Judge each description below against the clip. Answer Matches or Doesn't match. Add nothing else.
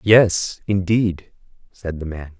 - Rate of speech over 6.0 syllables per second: Doesn't match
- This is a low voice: Matches